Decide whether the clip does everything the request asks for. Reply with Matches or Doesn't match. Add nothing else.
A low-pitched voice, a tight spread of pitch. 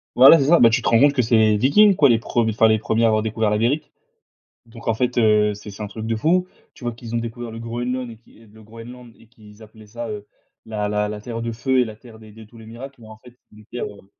Matches